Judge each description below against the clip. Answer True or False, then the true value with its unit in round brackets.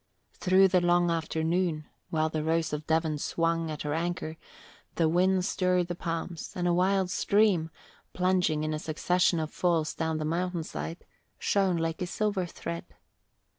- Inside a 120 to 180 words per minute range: True (160 wpm)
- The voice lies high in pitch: False (170 Hz)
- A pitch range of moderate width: False (2.3 semitones)